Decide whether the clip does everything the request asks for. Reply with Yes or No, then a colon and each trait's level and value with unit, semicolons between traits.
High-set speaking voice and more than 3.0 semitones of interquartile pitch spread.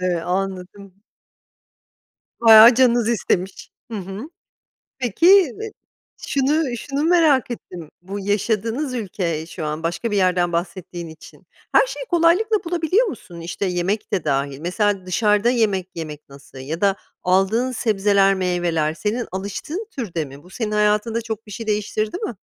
Yes: high, 205 Hz; average, 5.2 semitones